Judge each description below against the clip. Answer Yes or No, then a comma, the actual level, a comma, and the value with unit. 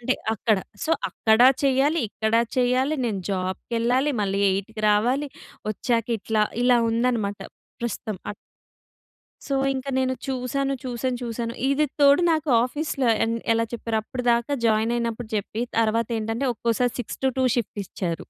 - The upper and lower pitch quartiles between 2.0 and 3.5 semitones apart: Yes, average, 3.0 semitones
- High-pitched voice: Yes, high, 235 Hz